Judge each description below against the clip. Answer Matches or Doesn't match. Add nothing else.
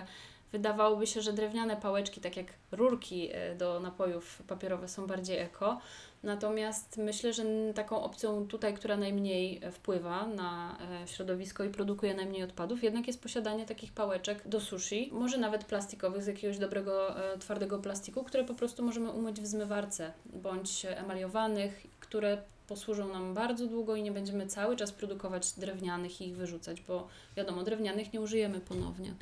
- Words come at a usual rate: Matches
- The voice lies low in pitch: Doesn't match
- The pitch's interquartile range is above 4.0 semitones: Doesn't match